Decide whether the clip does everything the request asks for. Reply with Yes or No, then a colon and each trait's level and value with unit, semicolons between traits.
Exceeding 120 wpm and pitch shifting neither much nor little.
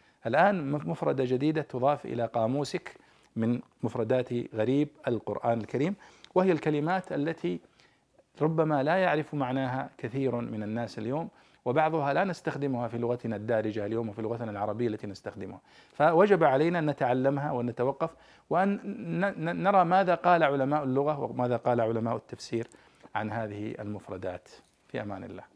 Yes: average, 130 wpm; average, 5.0 semitones